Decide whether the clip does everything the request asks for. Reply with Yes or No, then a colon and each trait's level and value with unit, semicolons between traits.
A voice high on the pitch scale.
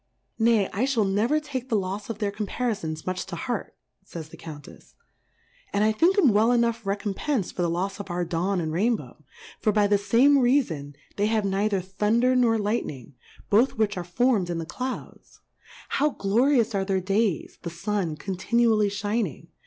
Yes: high, 205 Hz